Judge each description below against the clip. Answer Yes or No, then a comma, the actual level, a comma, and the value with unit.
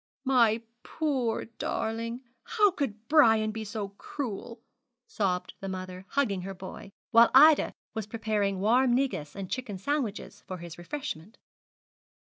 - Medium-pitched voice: No, high, 220 Hz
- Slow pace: Yes, slow, 130 wpm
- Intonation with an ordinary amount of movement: Yes, average, 4.8 semitones